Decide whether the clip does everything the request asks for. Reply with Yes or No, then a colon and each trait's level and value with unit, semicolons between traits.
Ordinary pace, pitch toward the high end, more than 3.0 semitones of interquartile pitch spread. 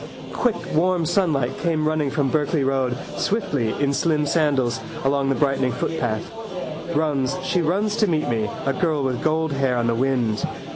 No: average, 165 wpm; medium, 145 Hz; average, 3.4 semitones